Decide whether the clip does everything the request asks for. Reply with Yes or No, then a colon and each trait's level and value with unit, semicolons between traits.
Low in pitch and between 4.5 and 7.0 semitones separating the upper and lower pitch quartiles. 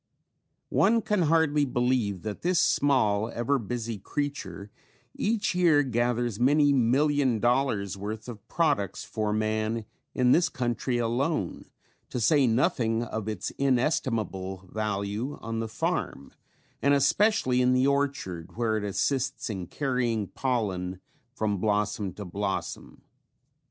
Yes: low, 120 Hz; average, 4.8 semitones